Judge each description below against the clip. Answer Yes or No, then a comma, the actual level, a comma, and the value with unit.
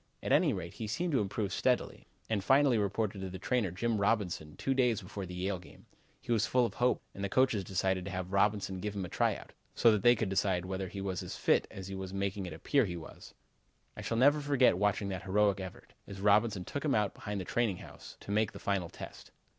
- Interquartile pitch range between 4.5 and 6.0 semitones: No, average, 3.2 semitones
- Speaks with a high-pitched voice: No, low, 100 Hz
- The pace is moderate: No, fast, 240 wpm